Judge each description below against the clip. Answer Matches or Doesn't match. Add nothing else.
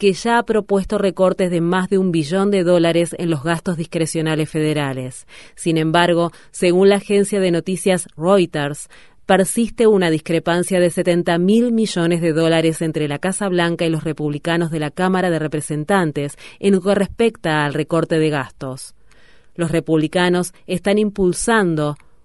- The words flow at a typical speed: Matches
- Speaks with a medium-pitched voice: Matches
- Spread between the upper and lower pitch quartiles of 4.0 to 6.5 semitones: Doesn't match